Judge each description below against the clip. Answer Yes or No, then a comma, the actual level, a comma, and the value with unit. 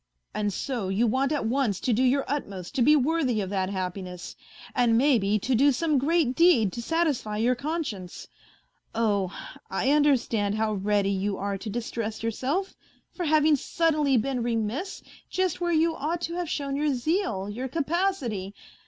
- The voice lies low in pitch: No, very high, 250 Hz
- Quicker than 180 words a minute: No, average, 170 wpm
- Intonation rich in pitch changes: Yes, wide, 6.4 semitones